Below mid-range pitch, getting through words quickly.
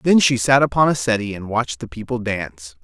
Yes: low, 115 Hz; fast, 235 wpm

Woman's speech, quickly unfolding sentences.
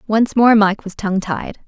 Yes: female; fast, 215 wpm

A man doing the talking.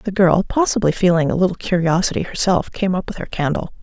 No: female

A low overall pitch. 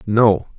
Yes: low, 105 Hz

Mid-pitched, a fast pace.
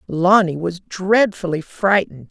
No: medium, 180 Hz; slow, 105 wpm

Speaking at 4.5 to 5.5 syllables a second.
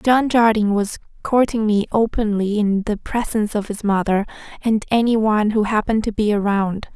Yes: 5.4 syllables/s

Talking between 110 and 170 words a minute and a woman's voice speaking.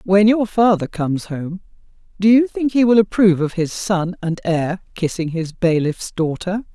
No: average, 180 wpm; female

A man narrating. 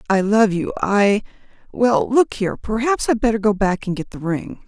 No: female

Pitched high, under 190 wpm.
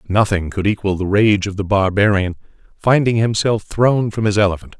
No: low, 100 Hz; average, 175 wpm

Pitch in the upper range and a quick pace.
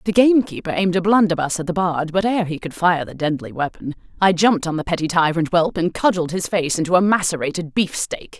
No: medium, 175 Hz; fast, 220 wpm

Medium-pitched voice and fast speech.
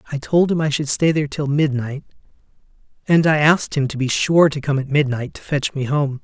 Yes: medium, 145 Hz; fast, 230 wpm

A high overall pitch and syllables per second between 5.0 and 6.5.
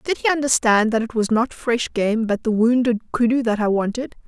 Yes: high, 230 Hz; 5.2 syllables/s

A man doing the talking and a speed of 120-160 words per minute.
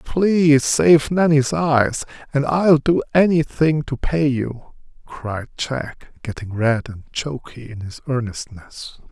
Yes: male; average, 140 wpm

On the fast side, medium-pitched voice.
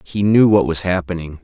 No: fast, 210 wpm; very low, 90 Hz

